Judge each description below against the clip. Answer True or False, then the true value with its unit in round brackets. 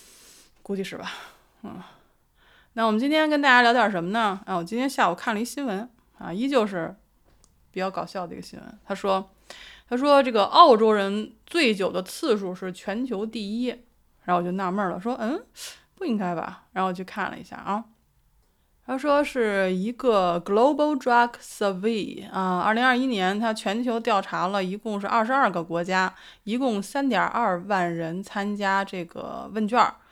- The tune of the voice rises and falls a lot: False (4.3 semitones)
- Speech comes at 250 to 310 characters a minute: True (280 characters per minute)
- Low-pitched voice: False (210 Hz)